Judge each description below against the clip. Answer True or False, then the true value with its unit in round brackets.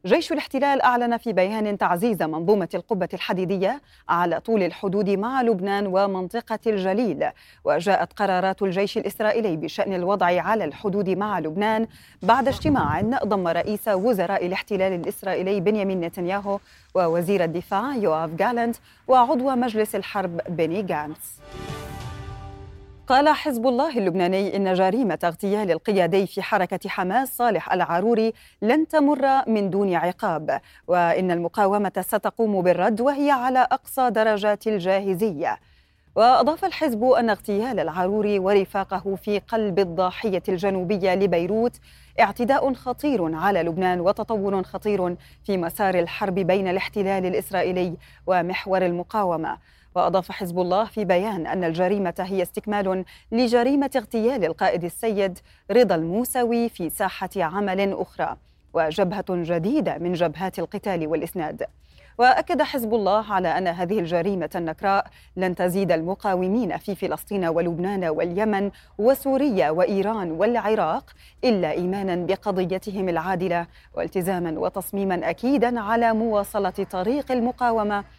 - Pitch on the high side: True (195 Hz)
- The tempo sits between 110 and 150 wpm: True (115 wpm)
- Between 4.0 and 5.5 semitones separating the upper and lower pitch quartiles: False (3.4 semitones)